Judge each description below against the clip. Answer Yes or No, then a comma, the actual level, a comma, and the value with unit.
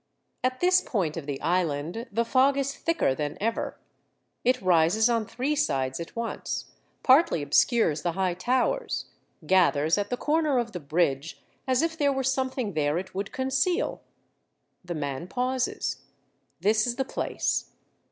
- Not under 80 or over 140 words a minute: No, average, 155 wpm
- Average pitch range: No, wide, 7.9 semitones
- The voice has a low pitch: No, high, 220 Hz